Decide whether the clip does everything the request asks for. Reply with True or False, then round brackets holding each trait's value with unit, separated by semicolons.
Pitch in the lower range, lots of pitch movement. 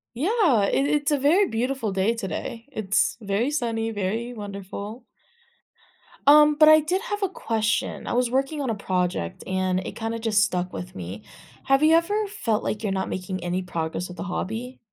False (225 Hz; 7.1 semitones)